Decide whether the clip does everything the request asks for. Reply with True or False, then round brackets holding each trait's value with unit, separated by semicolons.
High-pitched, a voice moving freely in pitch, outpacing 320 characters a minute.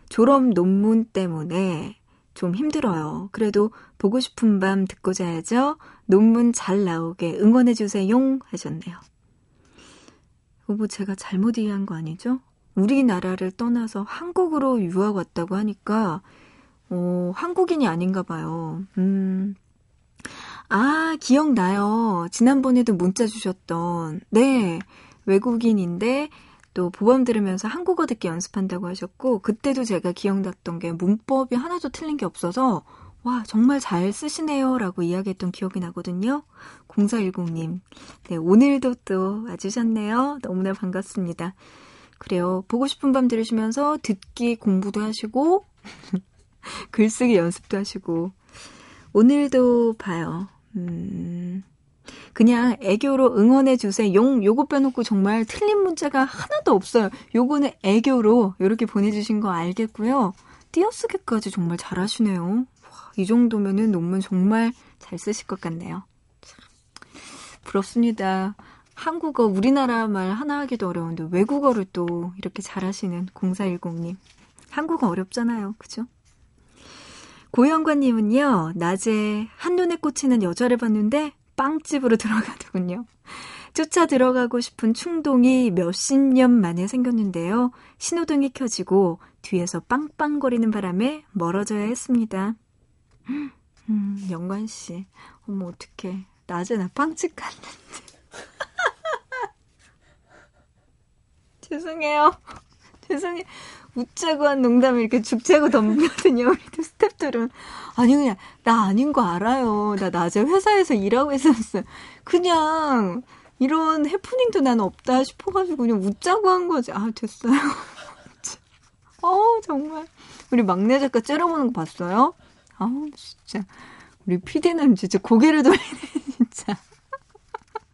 False (225 Hz; 5.9 semitones; 265 characters per minute)